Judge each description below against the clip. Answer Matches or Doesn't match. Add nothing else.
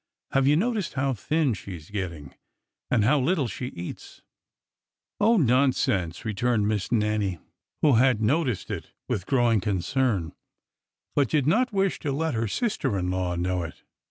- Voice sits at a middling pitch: Doesn't match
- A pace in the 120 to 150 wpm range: Doesn't match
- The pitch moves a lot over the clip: Matches